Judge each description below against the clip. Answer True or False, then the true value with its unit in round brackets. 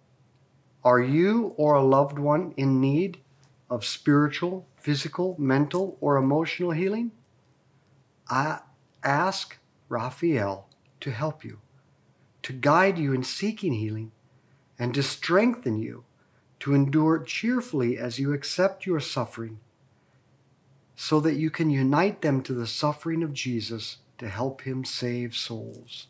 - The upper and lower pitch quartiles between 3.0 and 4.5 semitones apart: True (4.1 semitones)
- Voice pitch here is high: False (140 Hz)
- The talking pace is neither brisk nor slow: False (125 wpm)